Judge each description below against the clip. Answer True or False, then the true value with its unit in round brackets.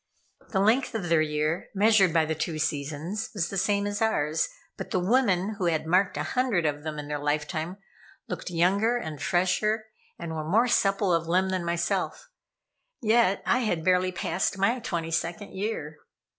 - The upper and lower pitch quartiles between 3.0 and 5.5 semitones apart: True (4.3 semitones)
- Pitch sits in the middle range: True (180 Hz)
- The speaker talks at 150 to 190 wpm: True (180 wpm)